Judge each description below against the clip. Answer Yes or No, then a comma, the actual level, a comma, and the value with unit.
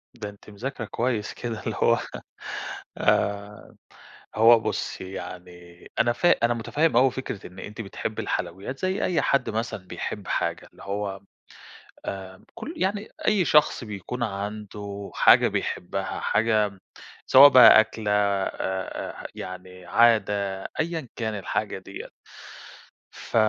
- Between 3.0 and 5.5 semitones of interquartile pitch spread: Yes, average, 3.6 semitones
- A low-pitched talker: Yes, low, 105 Hz